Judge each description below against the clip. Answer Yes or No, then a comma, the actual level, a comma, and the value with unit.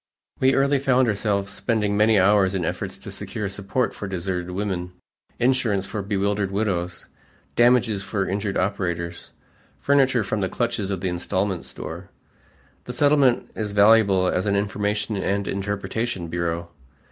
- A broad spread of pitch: No, average, 2.9 semitones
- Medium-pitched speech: No, low, 100 Hz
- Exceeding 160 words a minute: No, average, 145 wpm